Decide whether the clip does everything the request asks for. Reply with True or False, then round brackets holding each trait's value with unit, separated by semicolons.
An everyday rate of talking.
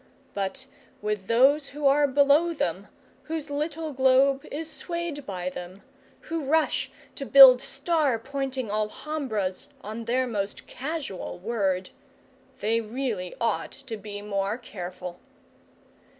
False (120 wpm)